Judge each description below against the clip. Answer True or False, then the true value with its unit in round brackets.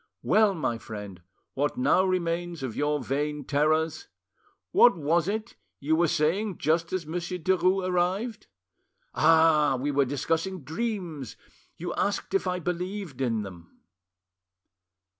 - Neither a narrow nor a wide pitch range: True (4.1 semitones)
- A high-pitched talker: False (165 Hz)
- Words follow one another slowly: True (130 wpm)